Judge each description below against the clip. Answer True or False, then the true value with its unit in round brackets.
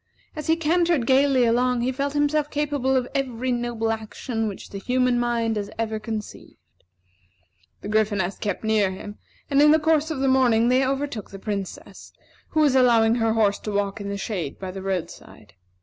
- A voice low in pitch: False (240 Hz)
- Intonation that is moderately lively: True (4.3 semitones)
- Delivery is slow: False (185 wpm)